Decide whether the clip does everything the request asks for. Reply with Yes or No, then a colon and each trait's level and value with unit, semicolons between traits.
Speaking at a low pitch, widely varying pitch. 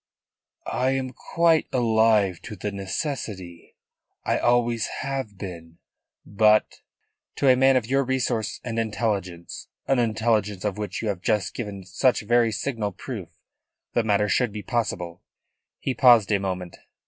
No: low, 110 Hz; average, 3.7 semitones